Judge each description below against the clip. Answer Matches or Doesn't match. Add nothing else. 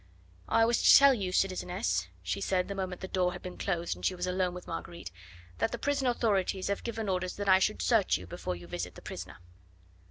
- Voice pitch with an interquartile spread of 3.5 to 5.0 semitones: Doesn't match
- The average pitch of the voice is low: Doesn't match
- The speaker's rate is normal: Doesn't match